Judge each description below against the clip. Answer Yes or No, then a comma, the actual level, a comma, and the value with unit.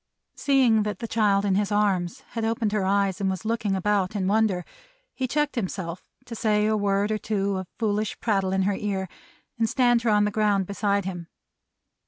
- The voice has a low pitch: No, high, 205 Hz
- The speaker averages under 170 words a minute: No, fast, 205 wpm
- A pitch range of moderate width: No, narrow, 2.3 semitones